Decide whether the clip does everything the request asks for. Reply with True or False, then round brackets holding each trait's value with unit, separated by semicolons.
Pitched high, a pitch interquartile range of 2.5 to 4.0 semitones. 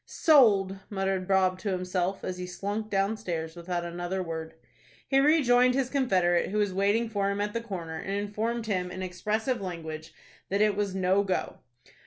True (195 Hz; 2.9 semitones)